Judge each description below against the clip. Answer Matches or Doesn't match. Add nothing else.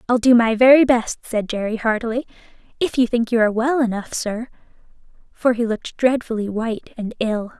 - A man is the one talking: Doesn't match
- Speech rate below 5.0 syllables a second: Doesn't match